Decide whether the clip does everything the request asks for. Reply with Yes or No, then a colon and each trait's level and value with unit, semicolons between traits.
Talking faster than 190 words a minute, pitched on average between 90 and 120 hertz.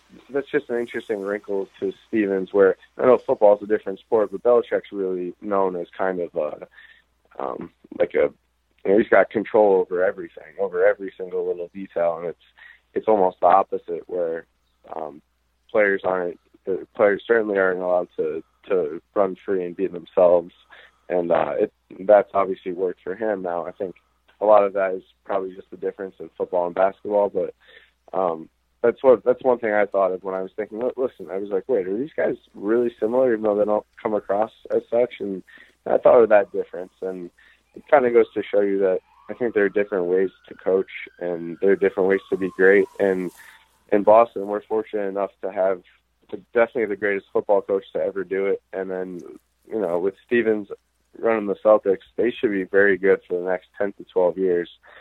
Yes: average, 200 wpm; low, 110 Hz